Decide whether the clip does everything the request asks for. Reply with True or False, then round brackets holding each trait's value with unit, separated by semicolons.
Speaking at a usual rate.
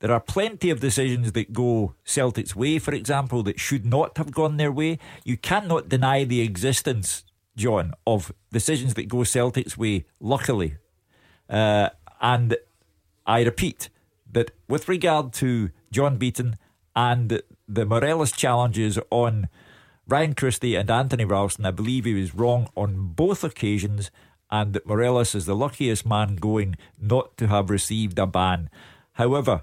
True (150 wpm)